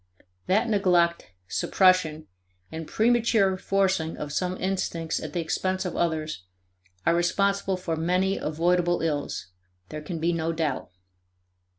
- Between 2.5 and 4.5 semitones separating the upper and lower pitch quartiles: Yes, average, 2.8 semitones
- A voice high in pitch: No, medium, 175 Hz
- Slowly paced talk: Yes, slow, 125 wpm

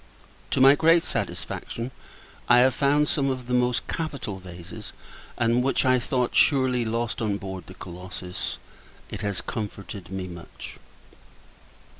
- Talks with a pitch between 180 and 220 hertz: No, low, 120 Hz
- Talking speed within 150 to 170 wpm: No, average, 140 wpm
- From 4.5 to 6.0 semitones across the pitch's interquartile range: Yes, average, 5.3 semitones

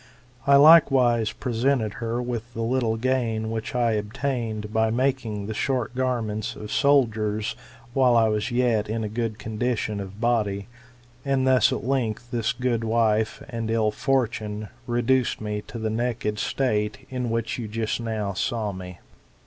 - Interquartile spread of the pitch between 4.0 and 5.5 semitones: No, narrow, 2.6 semitones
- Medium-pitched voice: No, low, 115 Hz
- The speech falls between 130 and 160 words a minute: Yes, average, 155 wpm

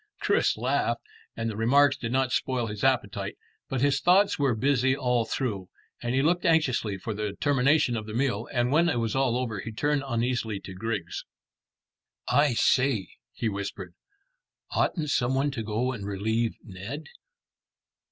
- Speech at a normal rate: Yes, average, 160 wpm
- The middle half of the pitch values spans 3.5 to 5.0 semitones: Yes, average, 3.9 semitones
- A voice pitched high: No, low, 120 Hz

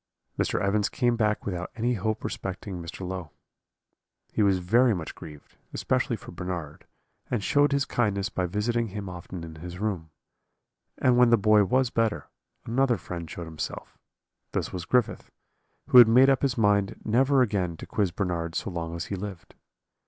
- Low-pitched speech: Yes, low, 100 Hz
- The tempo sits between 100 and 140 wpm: No, average, 175 wpm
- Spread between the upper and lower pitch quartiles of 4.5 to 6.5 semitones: Yes, average, 4.9 semitones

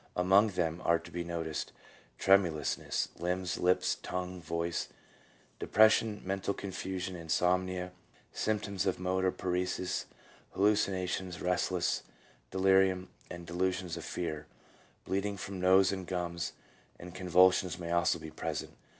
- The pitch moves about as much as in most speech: No, narrow, 1.6 semitones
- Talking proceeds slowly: Yes, slow, 120 wpm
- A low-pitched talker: Yes, very low, 90 Hz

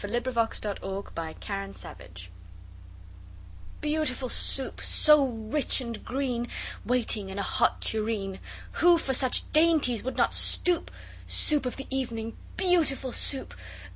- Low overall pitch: No, high, 245 Hz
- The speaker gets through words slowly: Yes, slow, 125 wpm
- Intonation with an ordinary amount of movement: Yes, average, 4.5 semitones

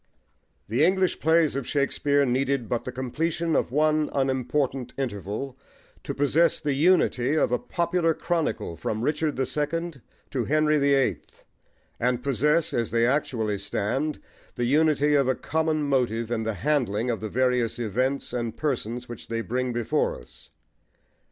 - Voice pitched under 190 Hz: Yes, low, 135 Hz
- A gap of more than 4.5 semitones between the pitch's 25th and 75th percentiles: No, average, 4.1 semitones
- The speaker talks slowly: No, average, 155 wpm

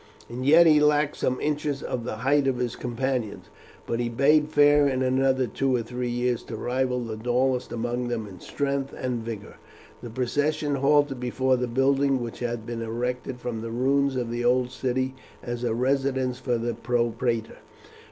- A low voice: Yes, low, 125 Hz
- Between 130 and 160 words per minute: No, average, 180 wpm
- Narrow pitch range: Yes, narrow, 2.2 semitones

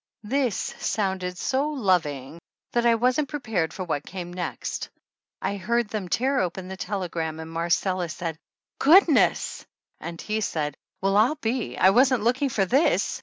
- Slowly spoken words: No, average, 160 wpm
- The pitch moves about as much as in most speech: No, wide, 6.0 semitones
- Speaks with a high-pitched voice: Yes, high, 195 Hz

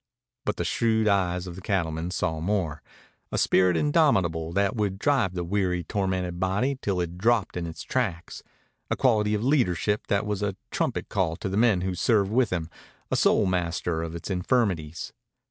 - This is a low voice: Yes, very low, 95 Hz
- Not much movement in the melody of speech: No, average, 3.3 semitones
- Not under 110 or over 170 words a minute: No, average, 180 wpm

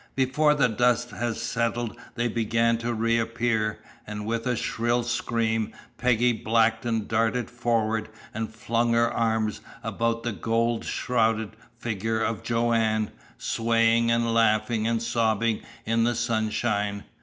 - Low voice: Yes, low, 115 Hz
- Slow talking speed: Yes, slow, 130 wpm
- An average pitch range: No, narrow, 1.0 semitones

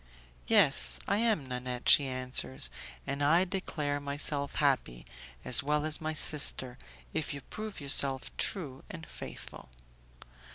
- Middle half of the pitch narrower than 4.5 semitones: Yes, average, 3.4 semitones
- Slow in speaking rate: Yes, slow, 130 wpm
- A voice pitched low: No, medium, 145 Hz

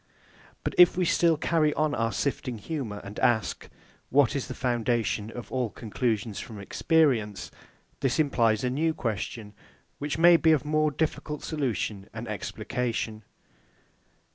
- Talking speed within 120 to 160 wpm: Yes, average, 140 wpm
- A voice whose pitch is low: Yes, low, 125 Hz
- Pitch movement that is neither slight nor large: No, wide, 5.7 semitones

